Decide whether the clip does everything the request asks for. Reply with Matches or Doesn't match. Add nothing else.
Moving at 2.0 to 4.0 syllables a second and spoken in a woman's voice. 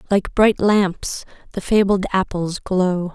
Matches